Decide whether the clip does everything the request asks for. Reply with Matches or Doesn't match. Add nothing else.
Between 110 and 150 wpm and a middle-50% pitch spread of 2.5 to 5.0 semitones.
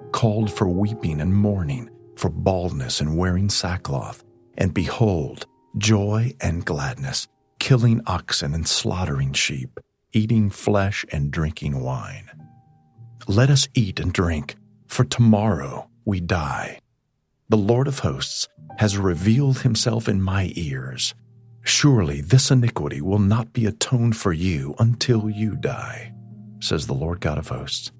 Matches